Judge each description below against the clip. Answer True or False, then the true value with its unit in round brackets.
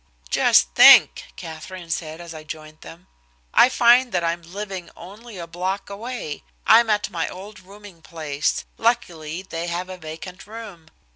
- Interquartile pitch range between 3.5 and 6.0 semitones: True (3.9 semitones)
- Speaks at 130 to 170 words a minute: True (155 wpm)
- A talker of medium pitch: True (180 Hz)